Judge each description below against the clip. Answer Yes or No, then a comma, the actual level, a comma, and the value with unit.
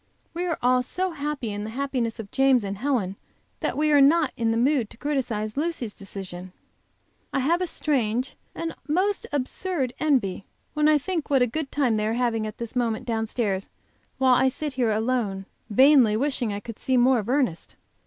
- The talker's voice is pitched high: Yes, very high, 250 Hz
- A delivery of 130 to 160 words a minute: No, average, 195 wpm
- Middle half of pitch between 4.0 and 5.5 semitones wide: Yes, average, 4.8 semitones